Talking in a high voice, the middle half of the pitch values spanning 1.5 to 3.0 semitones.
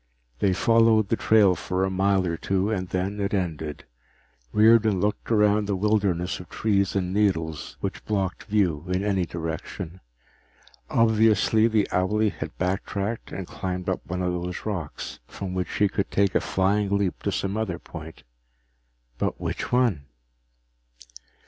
No: very low, 95 Hz; narrow, 2.6 semitones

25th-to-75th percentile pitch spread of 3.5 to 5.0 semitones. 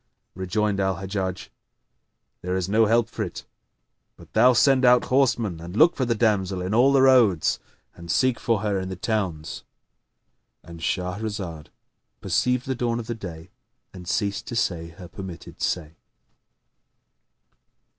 Yes: average, 4.6 semitones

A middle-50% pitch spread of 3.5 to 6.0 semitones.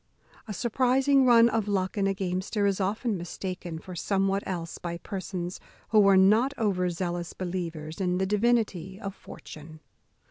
No: average, 3.0 semitones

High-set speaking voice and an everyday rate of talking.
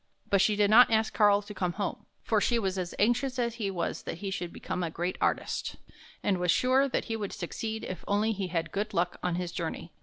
No: high, 200 Hz; fast, 240 wpm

